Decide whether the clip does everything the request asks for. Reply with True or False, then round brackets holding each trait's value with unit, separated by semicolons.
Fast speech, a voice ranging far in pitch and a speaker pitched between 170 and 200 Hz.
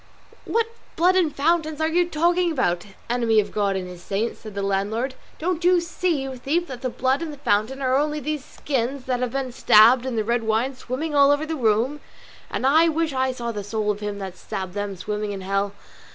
False (225 wpm; 6.3 semitones; 255 Hz)